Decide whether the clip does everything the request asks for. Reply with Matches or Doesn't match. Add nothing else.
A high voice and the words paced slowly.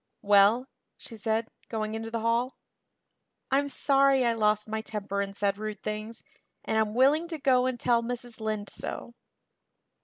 Doesn't match